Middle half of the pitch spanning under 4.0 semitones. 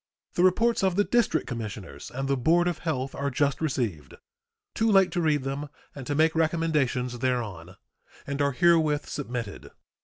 No: average, 4.9 semitones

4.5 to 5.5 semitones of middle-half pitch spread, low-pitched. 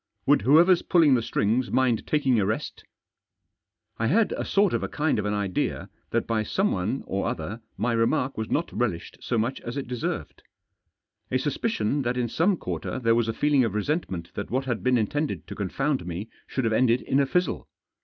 Yes: average, 4.8 semitones; low, 125 Hz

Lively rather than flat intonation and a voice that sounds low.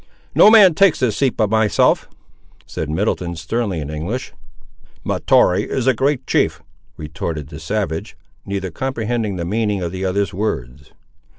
Yes: wide, 6.0 semitones; low, 100 Hz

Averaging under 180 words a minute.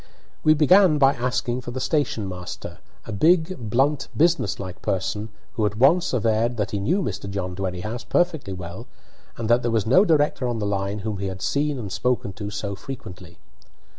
No: average, 185 wpm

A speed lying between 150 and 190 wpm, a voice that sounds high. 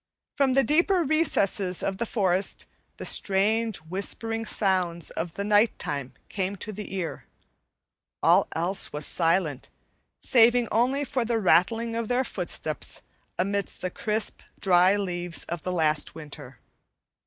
No: slow, 135 wpm; high, 200 Hz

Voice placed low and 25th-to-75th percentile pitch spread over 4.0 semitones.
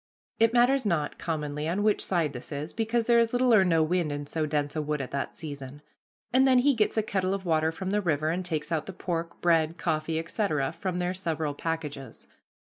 No: medium, 165 Hz; average, 4.6 semitones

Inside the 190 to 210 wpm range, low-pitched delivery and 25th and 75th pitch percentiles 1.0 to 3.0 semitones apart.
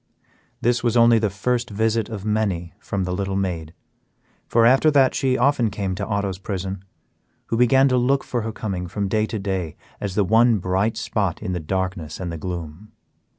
No: average, 195 wpm; low, 100 Hz; average, 3.7 semitones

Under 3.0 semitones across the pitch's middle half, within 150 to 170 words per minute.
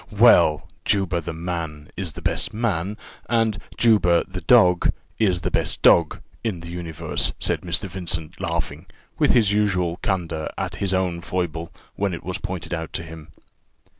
Yes: narrow, 2.6 semitones; average, 165 wpm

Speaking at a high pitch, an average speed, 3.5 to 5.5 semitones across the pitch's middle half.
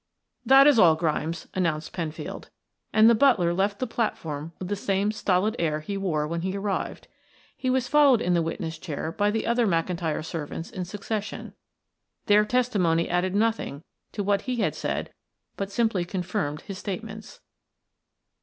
Yes: high, 195 Hz; average, 165 wpm; average, 4.5 semitones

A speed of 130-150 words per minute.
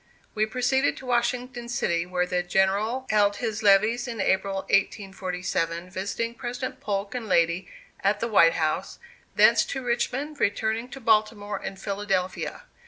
Yes: average, 145 wpm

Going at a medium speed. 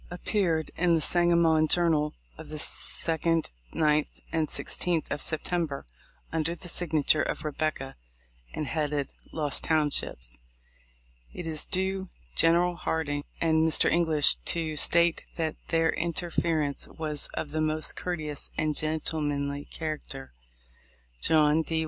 No: slow, 125 wpm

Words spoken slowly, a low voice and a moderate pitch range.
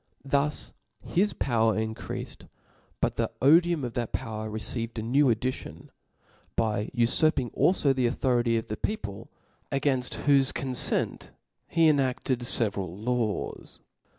Yes: slow, 125 wpm; low, 125 Hz; average, 3.7 semitones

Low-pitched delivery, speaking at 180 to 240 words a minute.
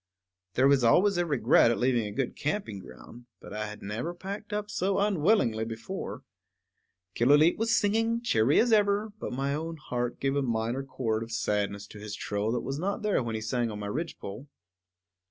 Yes: low, 130 Hz; average, 190 wpm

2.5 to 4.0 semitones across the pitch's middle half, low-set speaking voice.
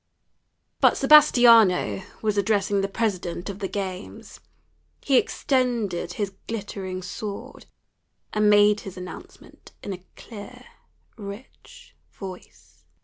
No: average, 2.8 semitones; high, 205 Hz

